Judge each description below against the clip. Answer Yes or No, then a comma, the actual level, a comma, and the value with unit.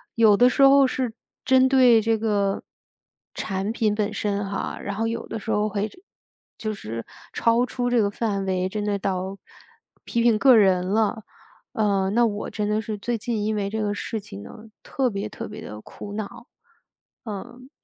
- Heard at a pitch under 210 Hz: No, high, 215 Hz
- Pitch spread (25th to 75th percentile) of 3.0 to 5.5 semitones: No, narrow, 2.4 semitones